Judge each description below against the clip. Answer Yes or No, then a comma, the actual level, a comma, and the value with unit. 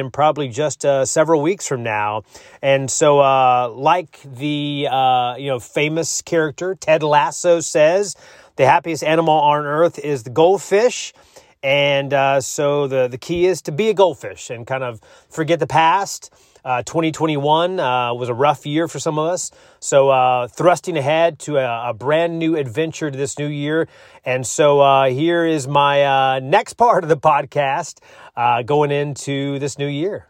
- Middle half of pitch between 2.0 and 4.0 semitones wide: Yes, average, 3.1 semitones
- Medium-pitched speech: Yes, medium, 145 Hz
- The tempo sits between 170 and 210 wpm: Yes, average, 175 wpm